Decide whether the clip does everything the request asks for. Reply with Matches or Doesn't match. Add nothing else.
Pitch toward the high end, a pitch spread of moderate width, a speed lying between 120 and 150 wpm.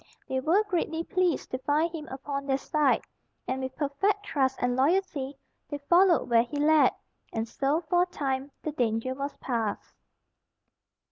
Doesn't match